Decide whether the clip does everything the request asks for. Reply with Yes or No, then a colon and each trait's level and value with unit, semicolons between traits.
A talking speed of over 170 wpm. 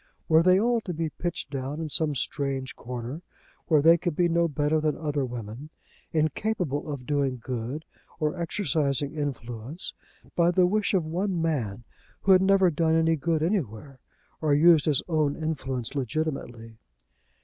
No: average, 160 wpm